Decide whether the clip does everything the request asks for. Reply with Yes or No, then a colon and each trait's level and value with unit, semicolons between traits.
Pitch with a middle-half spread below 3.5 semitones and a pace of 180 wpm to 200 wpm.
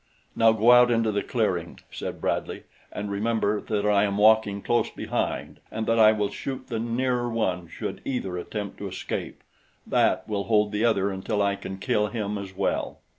Yes: narrow, 2.4 semitones; average, 185 wpm